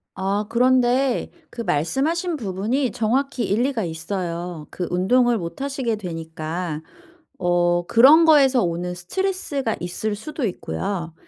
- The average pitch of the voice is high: Yes, high, 210 Hz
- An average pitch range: No, wide, 6.8 semitones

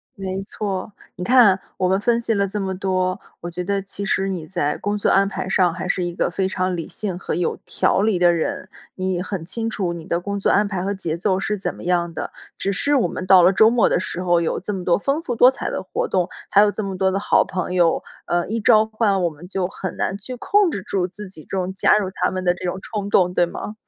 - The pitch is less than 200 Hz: Yes, high, 190 Hz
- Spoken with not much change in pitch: Yes, narrow, 2.3 semitones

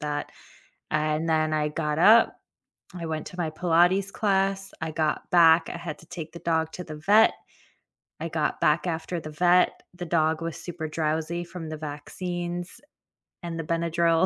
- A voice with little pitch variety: Yes, narrow, 2.0 semitones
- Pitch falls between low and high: Yes, medium, 165 Hz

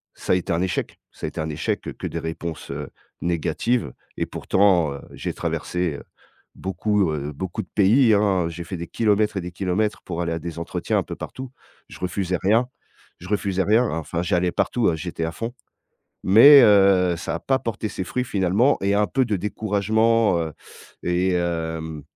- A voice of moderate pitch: No, very low, 95 Hz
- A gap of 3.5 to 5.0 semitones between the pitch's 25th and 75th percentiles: Yes, average, 4.0 semitones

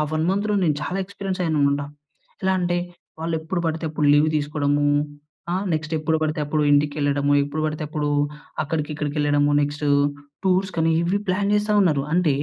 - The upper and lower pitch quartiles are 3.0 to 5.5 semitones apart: Yes, average, 3.5 semitones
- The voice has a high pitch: No, medium, 155 Hz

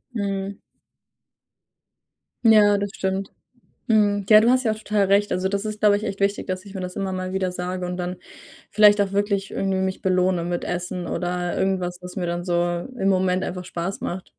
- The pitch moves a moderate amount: No, narrow, 2.0 semitones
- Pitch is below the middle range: No, high, 190 Hz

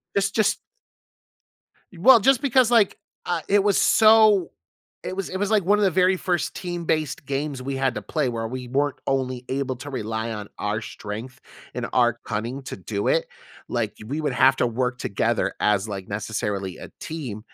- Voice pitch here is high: No, low, 135 Hz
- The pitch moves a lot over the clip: Yes, wide, 8.6 semitones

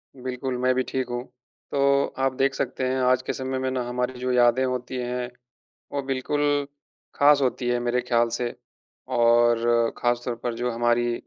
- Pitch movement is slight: Yes, narrow, 1.4 semitones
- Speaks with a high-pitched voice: No, low, 125 Hz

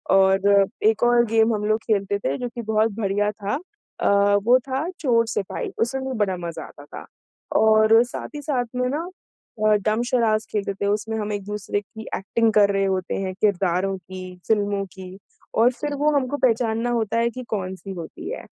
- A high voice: Yes, high, 215 Hz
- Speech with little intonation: No, average, 3.1 semitones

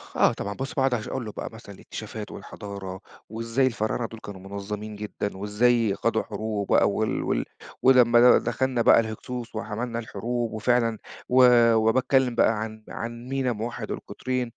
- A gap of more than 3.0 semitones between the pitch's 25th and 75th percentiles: No, narrow, 2.5 semitones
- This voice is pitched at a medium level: No, low, 115 Hz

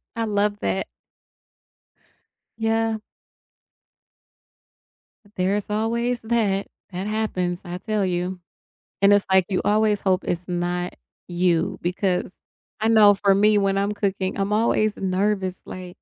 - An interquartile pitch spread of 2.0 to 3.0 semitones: Yes, narrow, 2.6 semitones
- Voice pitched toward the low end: No, high, 200 Hz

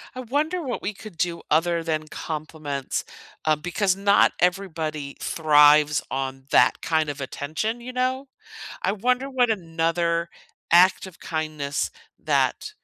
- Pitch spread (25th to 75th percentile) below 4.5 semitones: No, wide, 5.5 semitones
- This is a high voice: No, medium, 170 Hz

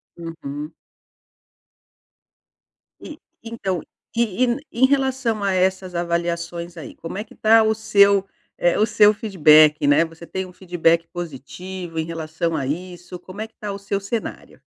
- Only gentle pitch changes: No, average, 4.0 semitones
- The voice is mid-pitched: Yes, medium, 180 Hz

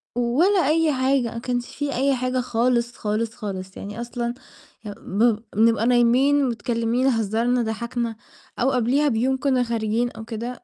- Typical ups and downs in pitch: No, narrow, 2.3 semitones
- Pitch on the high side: Yes, high, 240 Hz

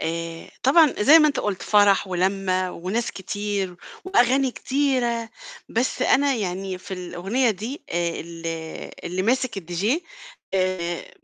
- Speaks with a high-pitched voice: Yes, high, 195 Hz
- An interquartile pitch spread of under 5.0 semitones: No, wide, 5.5 semitones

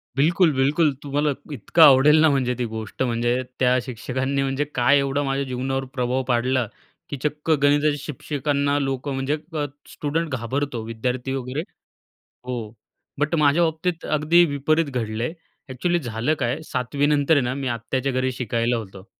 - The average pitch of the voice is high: No, low, 135 Hz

